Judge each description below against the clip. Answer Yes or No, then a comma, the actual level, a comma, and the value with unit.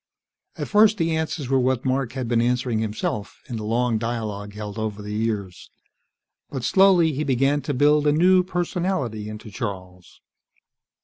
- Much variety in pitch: Yes, wide, 5.7 semitones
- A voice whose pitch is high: No, low, 125 Hz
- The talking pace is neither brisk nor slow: Yes, average, 165 wpm